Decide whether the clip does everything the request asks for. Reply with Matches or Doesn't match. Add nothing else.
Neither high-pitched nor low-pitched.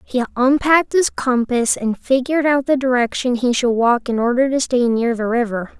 Doesn't match